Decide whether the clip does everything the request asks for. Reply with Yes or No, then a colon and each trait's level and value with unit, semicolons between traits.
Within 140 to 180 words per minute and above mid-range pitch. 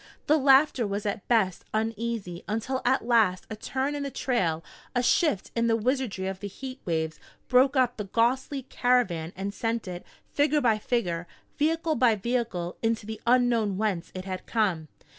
Yes: average, 175 wpm; high, 230 Hz